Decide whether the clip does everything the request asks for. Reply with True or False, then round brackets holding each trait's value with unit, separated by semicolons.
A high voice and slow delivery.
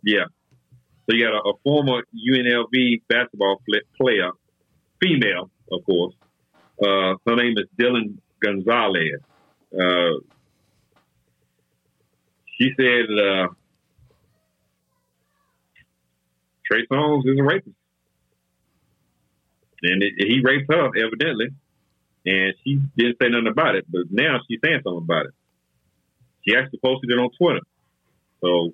False (105 Hz; 120 wpm)